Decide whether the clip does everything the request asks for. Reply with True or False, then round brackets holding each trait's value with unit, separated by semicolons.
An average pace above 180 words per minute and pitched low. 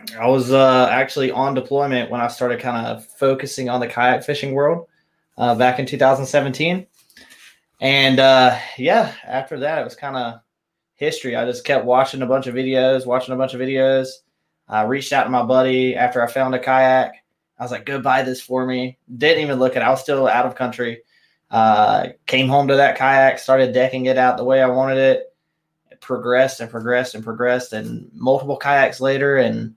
True (200 wpm; 130 Hz)